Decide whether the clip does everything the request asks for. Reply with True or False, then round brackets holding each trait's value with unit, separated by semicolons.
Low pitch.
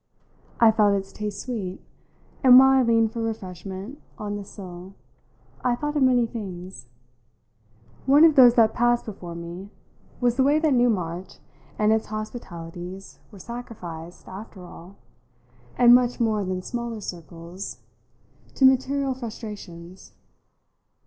False (215 Hz)